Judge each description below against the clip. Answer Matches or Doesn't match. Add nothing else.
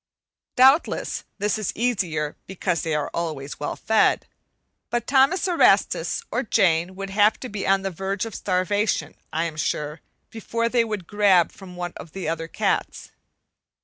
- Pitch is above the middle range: Matches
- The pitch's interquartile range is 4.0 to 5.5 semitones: Matches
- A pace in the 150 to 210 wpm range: Matches